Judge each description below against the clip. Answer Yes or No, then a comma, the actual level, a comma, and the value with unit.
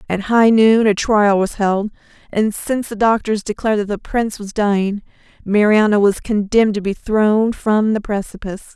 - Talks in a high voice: Yes, high, 210 Hz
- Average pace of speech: Yes, average, 180 wpm